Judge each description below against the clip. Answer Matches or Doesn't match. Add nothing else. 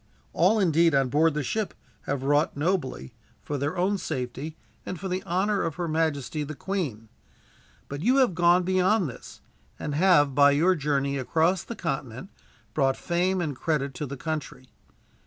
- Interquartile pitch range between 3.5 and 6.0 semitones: Matches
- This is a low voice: Doesn't match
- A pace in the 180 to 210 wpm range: Doesn't match